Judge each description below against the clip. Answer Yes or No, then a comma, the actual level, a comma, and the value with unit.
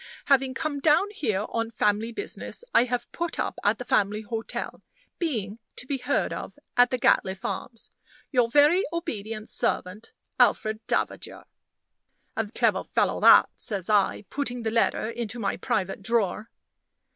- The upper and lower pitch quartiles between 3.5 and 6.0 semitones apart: Yes, average, 4.0 semitones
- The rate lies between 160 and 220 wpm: No, average, 150 wpm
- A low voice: No, high, 230 Hz